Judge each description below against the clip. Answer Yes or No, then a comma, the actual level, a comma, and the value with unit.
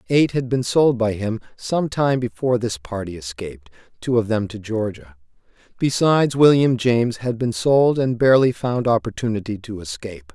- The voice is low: Yes, low, 115 Hz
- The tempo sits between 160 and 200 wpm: Yes, average, 170 wpm